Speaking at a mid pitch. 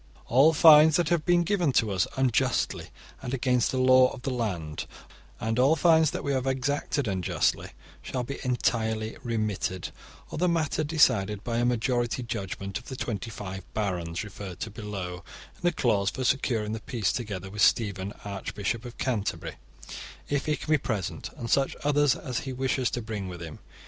No: low, 120 Hz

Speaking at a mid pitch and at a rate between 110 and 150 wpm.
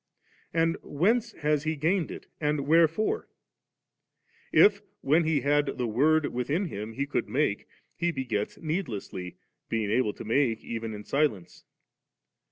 Yes: medium, 145 Hz; average, 140 wpm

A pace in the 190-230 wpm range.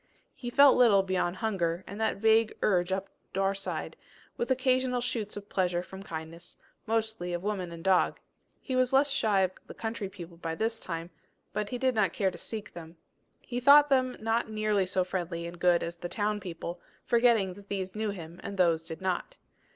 Yes: average, 195 wpm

